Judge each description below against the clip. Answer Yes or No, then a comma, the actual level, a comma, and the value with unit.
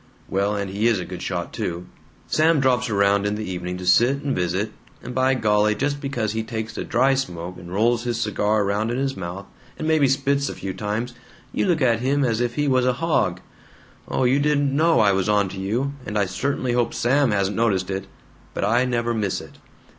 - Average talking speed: No, fast, 220 wpm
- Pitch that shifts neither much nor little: Yes, average, 4.8 semitones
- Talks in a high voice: No, low, 115 Hz